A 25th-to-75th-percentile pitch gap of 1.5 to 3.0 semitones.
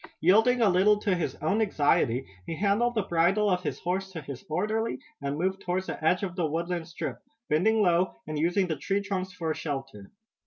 No: average, 4.0 semitones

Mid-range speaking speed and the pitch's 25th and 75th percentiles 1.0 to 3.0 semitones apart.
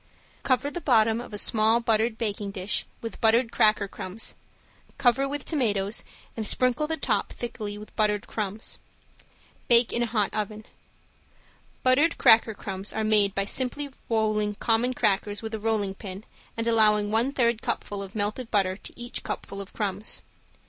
Yes: average, 160 wpm; narrow, 2.5 semitones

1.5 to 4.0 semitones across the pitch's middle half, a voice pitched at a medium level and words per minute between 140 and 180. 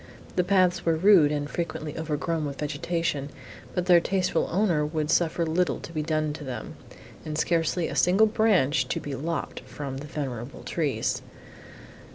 Yes: average, 3.1 semitones; medium, 160 Hz; average, 165 wpm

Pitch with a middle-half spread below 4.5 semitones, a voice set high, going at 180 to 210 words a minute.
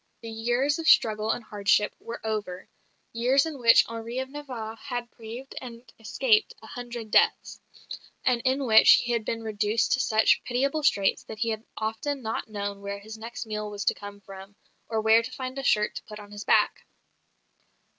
Yes: average, 2.9 semitones; high, 225 Hz; average, 190 wpm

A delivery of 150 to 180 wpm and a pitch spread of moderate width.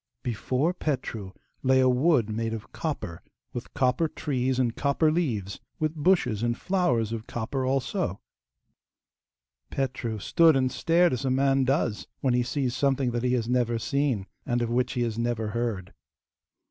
Yes: average, 160 wpm; average, 3.2 semitones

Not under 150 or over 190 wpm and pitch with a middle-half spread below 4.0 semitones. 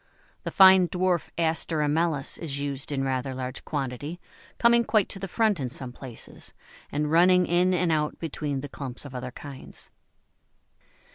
No: average, 160 wpm; average, 4.8 semitones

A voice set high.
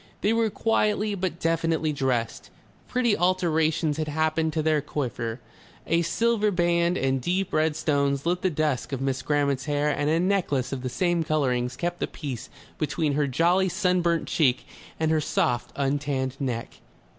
No: medium, 155 Hz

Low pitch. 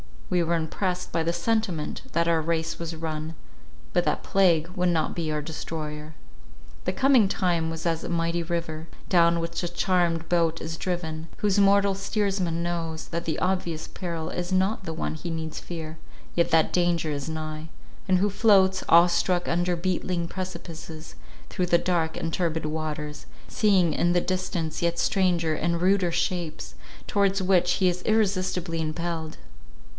No: medium, 170 Hz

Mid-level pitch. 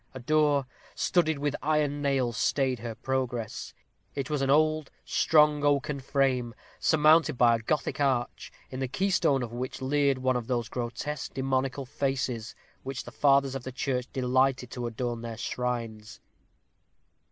No: low, 130 Hz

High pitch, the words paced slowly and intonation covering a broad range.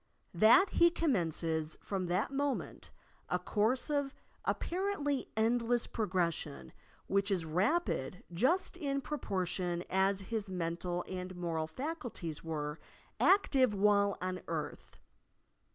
Yes: high, 195 Hz; slow, 110 wpm; wide, 7.3 semitones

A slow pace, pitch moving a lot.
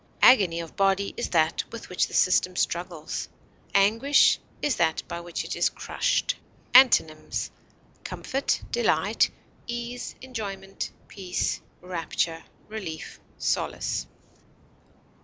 Yes: slow, 100 wpm; wide, 5.7 semitones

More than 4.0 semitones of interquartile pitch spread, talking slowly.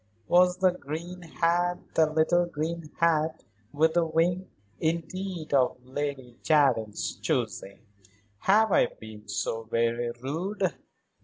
Yes: average, 4.6 semitones; slow, 120 wpm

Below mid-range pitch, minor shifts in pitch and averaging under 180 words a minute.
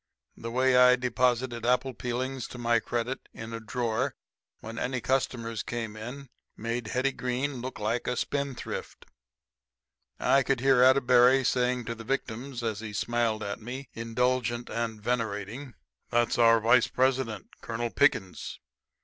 Yes: low, 120 Hz; narrow, 1.9 semitones; average, 140 wpm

